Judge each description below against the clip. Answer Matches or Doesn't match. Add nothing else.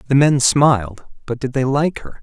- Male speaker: Matches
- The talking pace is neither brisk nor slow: Matches